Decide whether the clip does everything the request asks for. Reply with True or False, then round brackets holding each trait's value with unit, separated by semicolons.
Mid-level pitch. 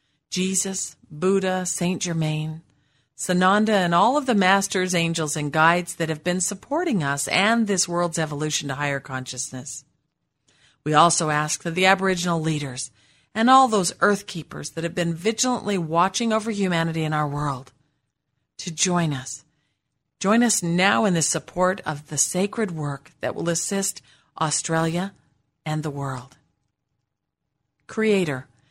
True (165 Hz)